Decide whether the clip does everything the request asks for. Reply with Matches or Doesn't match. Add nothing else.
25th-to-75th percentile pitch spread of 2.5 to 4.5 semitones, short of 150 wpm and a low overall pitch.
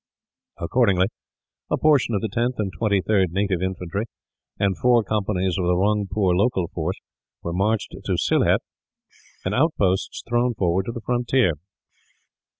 Matches